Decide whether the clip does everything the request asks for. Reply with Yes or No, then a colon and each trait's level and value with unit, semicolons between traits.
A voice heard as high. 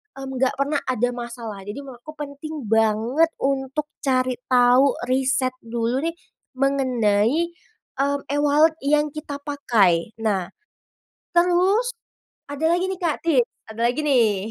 Yes: very high, 270 Hz